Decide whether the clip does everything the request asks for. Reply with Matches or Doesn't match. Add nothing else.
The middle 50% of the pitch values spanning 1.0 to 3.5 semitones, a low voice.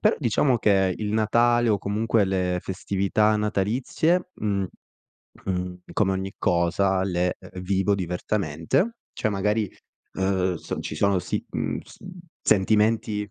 Matches